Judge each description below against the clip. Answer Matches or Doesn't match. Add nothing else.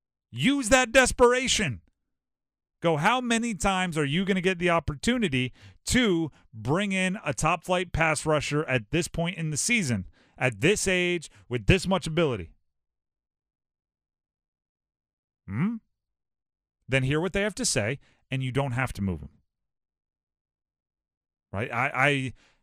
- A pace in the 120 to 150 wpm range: Matches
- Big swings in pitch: Matches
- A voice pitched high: Doesn't match